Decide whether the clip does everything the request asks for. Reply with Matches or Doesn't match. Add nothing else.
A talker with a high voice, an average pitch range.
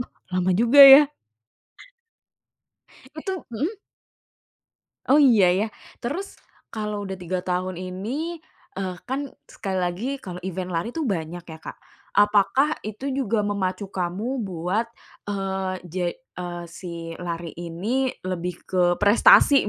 Doesn't match